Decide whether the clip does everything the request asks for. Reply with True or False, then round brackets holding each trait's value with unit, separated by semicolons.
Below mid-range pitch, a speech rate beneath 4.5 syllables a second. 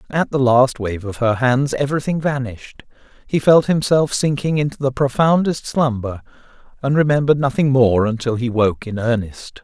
False (130 Hz; 5.4 syllables/s)